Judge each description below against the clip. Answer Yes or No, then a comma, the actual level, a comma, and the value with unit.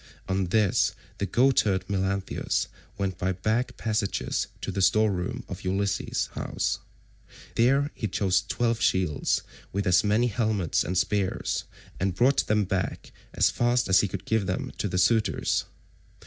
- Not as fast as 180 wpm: Yes, average, 155 wpm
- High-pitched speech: No, low, 100 Hz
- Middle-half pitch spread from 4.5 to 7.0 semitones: No, average, 2.9 semitones